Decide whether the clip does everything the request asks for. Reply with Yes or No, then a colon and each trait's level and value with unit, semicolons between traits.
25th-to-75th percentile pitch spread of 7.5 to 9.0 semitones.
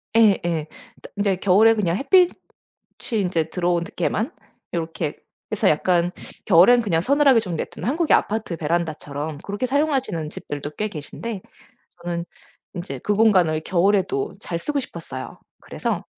No: average, 5.3 semitones